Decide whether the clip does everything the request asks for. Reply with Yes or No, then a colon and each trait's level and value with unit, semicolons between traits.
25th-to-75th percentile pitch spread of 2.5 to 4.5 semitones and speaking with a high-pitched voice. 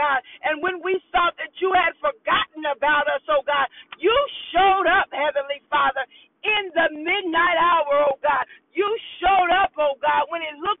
Yes: average, 4.1 semitones; very high, 320 Hz